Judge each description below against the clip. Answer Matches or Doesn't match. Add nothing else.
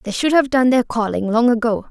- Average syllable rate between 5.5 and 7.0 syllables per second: Matches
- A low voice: Doesn't match